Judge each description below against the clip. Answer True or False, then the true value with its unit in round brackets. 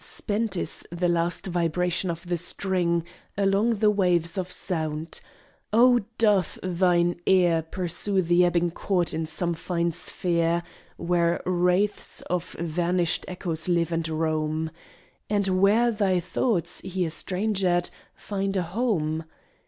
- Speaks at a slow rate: True (130 wpm)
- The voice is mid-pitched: True (175 Hz)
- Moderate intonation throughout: False (2.2 semitones)